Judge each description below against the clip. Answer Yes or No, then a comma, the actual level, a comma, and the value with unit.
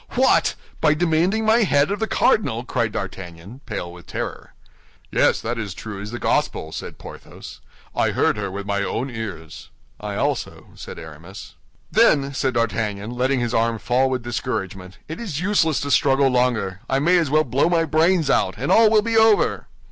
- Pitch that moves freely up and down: Yes, wide, 7.5 semitones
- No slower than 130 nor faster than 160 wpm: No, average, 185 wpm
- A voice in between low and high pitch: No, low, 125 Hz